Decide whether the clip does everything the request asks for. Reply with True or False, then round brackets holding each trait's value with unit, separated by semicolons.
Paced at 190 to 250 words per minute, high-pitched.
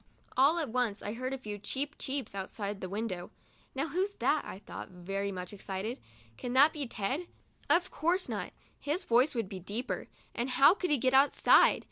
True (200 wpm; 250 Hz)